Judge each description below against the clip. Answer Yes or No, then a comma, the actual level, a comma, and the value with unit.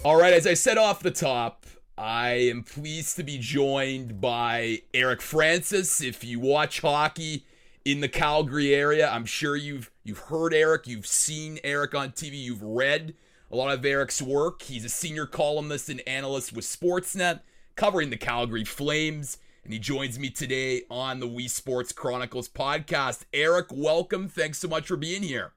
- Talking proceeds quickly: No, average, 175 wpm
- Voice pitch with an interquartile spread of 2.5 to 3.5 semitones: No, average, 4.0 semitones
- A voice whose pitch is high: No, medium, 140 Hz